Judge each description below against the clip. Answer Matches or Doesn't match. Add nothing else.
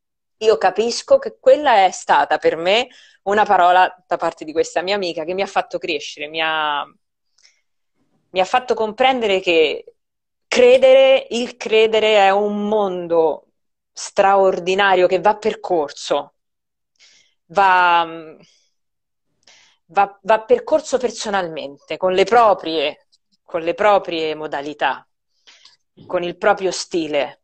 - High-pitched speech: Matches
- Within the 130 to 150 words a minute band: Doesn't match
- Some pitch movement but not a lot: Matches